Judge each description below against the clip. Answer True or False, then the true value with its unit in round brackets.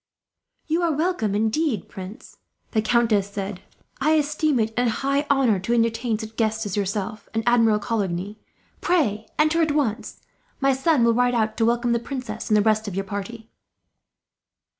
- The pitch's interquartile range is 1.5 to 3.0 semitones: False (4.2 semitones)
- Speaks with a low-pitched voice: False (230 Hz)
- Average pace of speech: True (170 wpm)